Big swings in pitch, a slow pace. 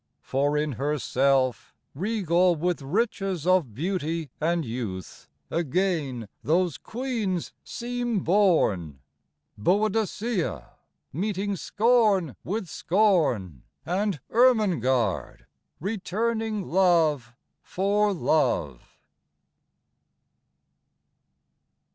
Yes: wide, 6.8 semitones; slow, 75 wpm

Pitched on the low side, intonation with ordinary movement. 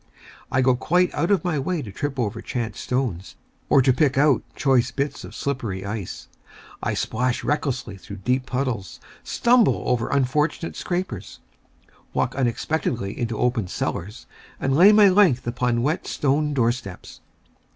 Yes: low, 130 Hz; average, 4.1 semitones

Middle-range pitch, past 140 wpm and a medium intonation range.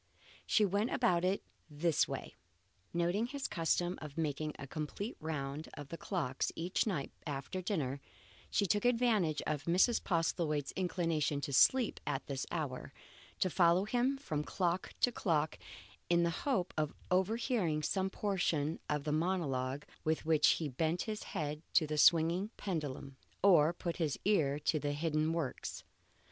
Yes: medium, 165 Hz; average, 155 wpm; average, 4.1 semitones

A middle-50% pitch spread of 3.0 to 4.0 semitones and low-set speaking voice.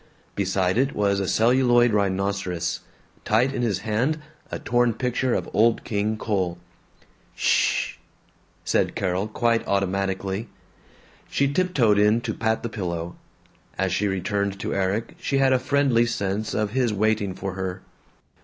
Yes: average, 3.6 semitones; low, 105 Hz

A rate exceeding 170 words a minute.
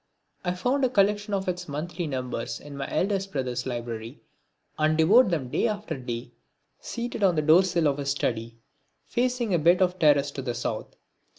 Yes: average, 180 wpm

